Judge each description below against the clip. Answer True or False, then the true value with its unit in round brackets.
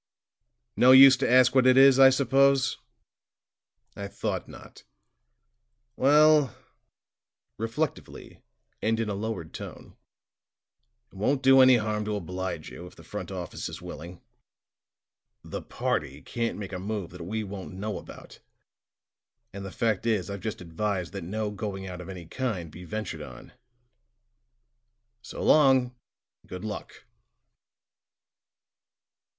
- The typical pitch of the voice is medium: False (105 Hz)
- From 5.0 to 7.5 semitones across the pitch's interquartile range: True (5.5 semitones)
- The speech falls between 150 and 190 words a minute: False (135 wpm)